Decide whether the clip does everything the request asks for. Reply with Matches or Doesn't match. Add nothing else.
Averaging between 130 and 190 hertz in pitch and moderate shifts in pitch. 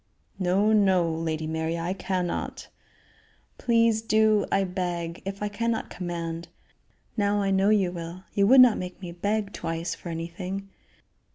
Matches